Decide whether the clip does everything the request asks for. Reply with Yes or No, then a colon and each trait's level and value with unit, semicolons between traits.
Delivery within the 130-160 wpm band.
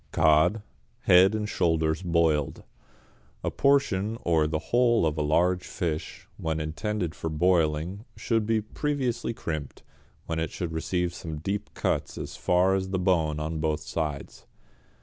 Yes: average, 150 wpm